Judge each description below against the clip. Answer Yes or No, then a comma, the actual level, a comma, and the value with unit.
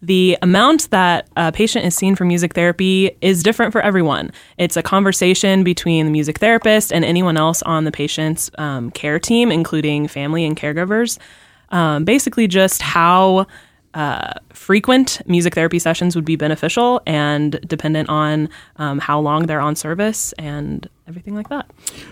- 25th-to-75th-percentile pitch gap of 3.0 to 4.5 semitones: Yes, average, 3.9 semitones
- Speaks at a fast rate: No, average, 160 wpm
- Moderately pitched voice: Yes, medium, 175 Hz